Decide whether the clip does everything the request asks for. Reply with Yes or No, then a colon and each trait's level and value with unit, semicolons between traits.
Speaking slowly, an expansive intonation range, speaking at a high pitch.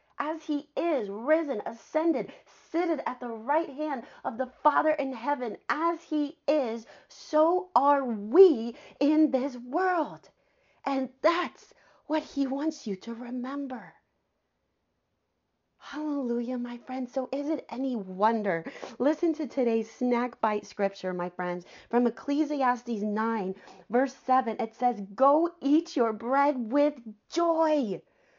No: slow, 130 wpm; average, 4.5 semitones; very high, 270 Hz